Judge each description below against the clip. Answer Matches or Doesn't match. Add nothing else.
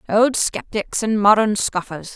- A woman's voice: Matches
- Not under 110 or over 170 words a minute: Matches